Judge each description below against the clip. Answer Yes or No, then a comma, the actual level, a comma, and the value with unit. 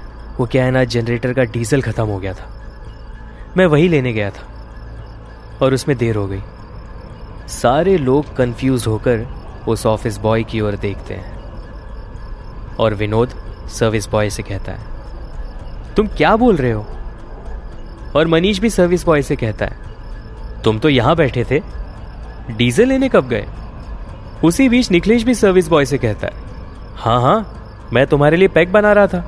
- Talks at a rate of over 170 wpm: No, average, 160 wpm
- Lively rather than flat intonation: Yes, wide, 5.9 semitones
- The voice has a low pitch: Yes, low, 115 Hz